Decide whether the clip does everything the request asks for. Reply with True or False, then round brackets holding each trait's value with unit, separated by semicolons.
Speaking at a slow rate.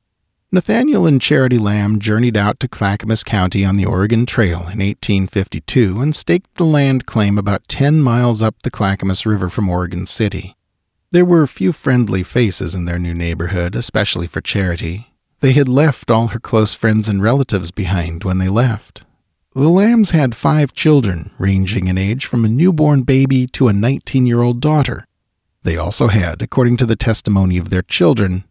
False (180 wpm)